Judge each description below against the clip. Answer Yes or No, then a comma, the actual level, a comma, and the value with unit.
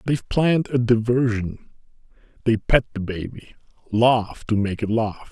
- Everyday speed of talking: Yes, average, 145 wpm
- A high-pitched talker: No, low, 115 Hz